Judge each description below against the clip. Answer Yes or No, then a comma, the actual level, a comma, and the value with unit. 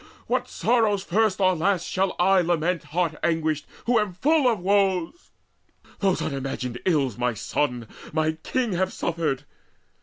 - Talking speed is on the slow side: No, average, 145 wpm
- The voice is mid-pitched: Yes, medium, 180 Hz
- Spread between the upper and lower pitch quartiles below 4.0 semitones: No, average, 4.3 semitones